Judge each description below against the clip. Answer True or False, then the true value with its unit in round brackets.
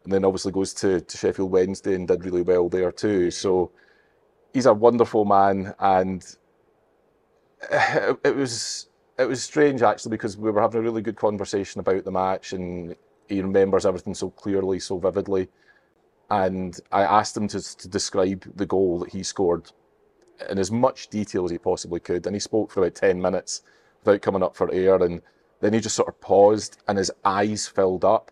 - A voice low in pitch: True (95 Hz)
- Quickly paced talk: False (190 wpm)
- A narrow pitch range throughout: True (2.2 semitones)